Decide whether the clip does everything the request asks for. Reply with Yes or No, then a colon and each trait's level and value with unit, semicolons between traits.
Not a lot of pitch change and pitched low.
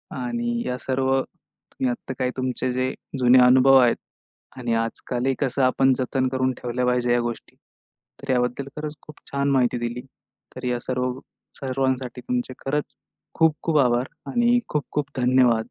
Yes: narrow, 1.6 semitones; low, 130 Hz